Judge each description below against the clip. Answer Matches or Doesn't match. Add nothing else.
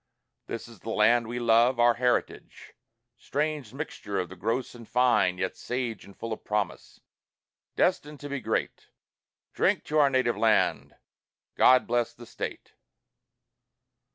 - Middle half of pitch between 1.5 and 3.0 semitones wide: Matches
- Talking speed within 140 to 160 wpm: Matches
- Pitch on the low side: Matches